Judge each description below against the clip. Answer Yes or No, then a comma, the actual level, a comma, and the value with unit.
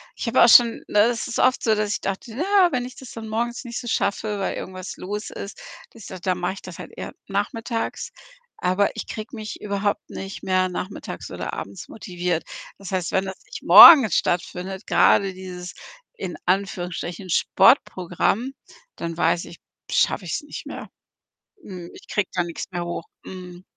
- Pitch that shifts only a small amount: No, average, 3.7 semitones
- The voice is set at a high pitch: Yes, high, 195 Hz